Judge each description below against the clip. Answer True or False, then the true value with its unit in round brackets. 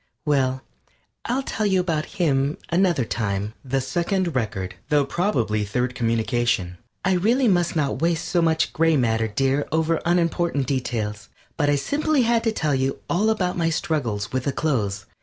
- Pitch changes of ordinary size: False (6.3 semitones)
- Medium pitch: True (145 Hz)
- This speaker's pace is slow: False (170 wpm)